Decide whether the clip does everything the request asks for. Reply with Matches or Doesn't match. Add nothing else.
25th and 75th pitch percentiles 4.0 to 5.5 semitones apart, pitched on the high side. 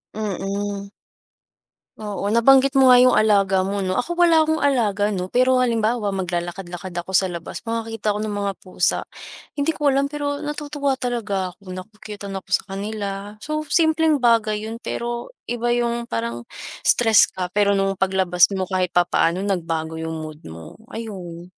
Matches